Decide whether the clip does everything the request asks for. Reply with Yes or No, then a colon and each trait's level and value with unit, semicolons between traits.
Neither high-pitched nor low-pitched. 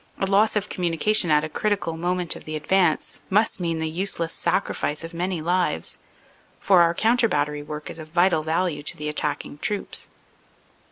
Yes: medium, 170 Hz